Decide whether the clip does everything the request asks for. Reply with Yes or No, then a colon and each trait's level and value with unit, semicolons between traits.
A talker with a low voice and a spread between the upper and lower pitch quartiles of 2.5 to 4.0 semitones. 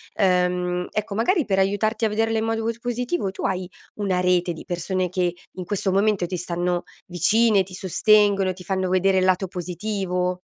No: high, 190 Hz; average, 2.9 semitones